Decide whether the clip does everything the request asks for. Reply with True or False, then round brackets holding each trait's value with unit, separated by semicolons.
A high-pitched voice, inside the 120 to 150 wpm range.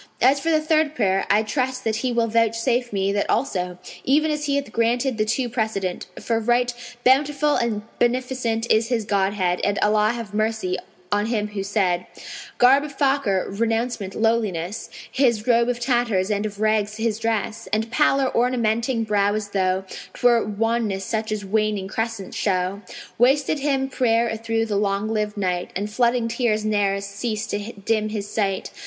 False (225 Hz; 175 wpm)